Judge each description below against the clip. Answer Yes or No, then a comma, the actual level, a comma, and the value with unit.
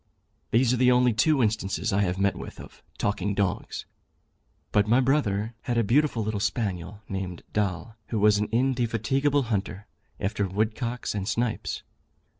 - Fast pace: No, average, 155 wpm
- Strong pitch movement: No, average, 3.4 semitones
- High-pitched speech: No, low, 110 Hz